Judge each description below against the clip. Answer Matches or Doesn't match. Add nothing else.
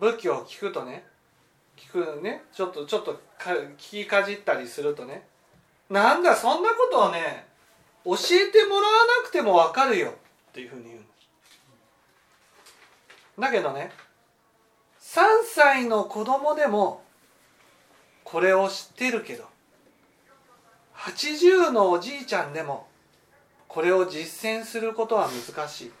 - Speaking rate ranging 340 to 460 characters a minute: Doesn't match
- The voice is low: Doesn't match